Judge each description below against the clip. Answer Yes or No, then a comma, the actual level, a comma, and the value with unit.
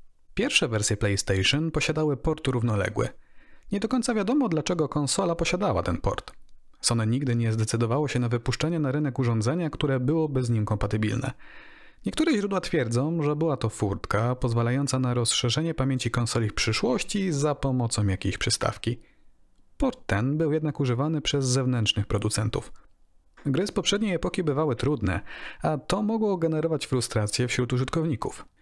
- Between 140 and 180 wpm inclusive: Yes, average, 145 wpm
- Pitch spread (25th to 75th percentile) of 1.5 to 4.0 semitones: No, wide, 5.4 semitones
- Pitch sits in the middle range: No, low, 130 Hz